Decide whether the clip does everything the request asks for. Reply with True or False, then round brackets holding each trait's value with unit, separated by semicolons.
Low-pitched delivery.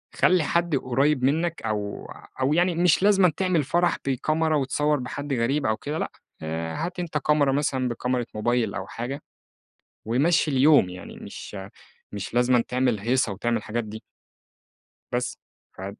True (130 Hz)